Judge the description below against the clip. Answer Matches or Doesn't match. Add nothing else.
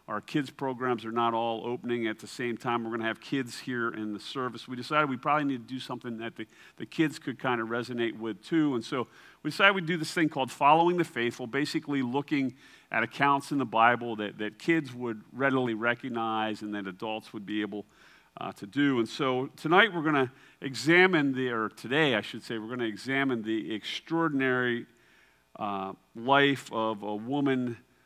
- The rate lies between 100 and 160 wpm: Doesn't match